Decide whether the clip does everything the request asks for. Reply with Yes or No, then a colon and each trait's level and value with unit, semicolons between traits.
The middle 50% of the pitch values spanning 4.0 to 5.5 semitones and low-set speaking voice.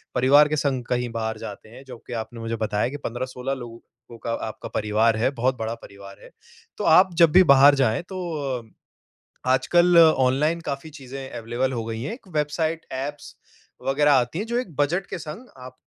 Yes: average, 4.5 semitones; low, 130 Hz